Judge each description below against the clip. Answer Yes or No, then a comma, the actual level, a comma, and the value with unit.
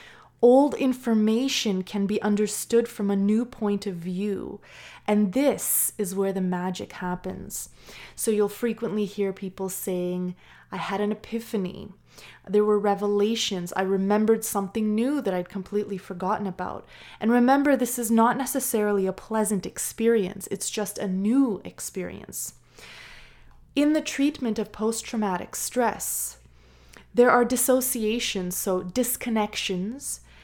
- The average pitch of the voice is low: No, high, 210 Hz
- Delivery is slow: Yes, slow, 130 wpm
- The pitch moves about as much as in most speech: Yes, average, 3.2 semitones